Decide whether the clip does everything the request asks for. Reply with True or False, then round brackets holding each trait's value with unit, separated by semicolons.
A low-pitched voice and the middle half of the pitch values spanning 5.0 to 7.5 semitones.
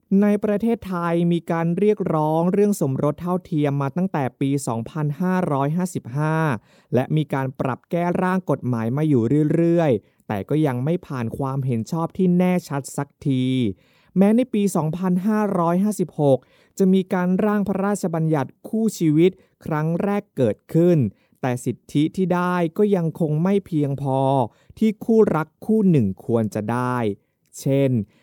False (160 Hz; 5.3 semitones)